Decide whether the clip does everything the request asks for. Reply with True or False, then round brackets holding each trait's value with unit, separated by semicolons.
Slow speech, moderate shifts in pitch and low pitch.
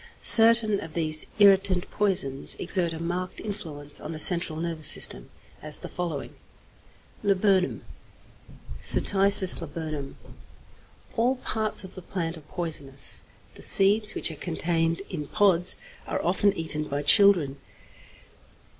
False (125 wpm; 4.2 semitones; 175 Hz)